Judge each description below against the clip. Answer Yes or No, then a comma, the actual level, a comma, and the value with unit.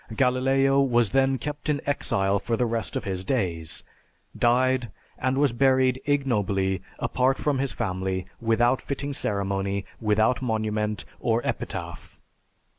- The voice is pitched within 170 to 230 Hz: No, low, 120 Hz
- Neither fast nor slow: No, slow, 130 wpm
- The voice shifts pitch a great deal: No, average, 4.8 semitones